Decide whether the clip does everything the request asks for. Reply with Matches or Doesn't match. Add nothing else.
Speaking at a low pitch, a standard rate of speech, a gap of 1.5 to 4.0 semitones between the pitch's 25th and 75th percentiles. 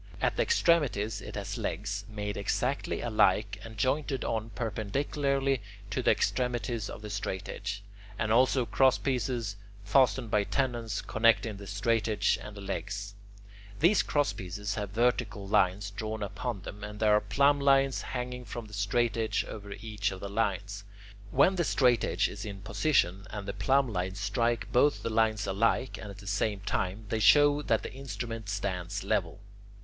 Matches